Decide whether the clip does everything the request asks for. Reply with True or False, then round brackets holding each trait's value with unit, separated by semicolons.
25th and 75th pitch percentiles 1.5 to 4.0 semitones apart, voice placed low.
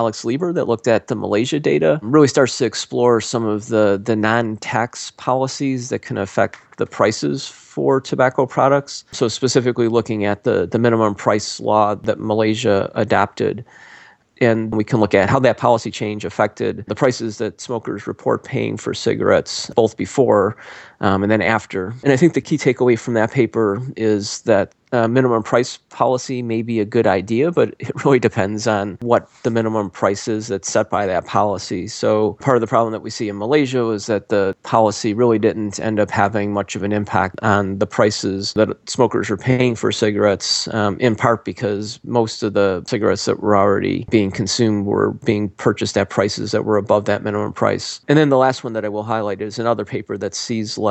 True (2.7 semitones; 110 Hz)